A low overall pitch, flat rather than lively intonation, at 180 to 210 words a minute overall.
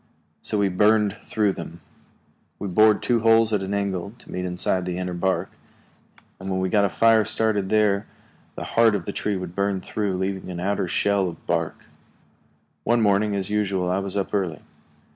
Yes: low, 100 Hz; narrow, 2.3 semitones; average, 190 wpm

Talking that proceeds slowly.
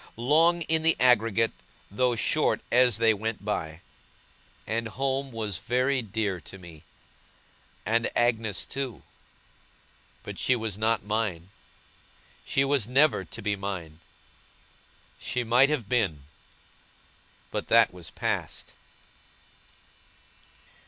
Yes: slow, 110 wpm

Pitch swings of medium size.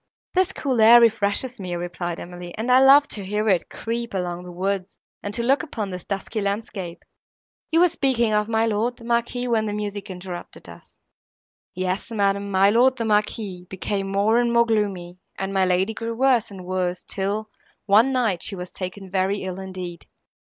Yes: average, 3.7 semitones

